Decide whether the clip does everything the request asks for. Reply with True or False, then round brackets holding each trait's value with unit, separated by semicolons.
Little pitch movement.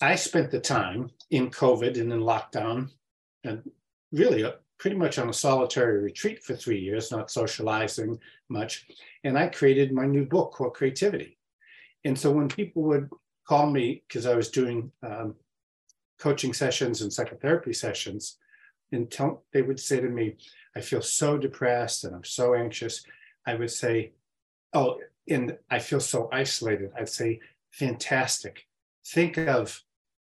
False (3.7 semitones)